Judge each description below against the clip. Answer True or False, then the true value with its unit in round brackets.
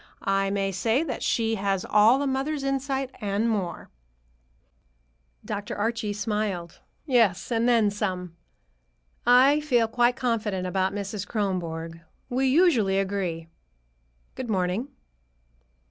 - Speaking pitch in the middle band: False (210 Hz)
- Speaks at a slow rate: True (115 wpm)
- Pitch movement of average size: True (4.2 semitones)